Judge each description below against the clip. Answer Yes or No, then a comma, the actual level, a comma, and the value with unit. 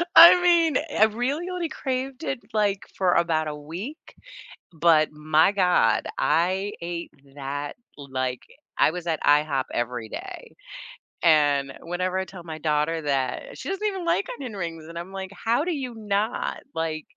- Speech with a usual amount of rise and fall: No, wide, 7.7 semitones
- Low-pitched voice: No, medium, 175 Hz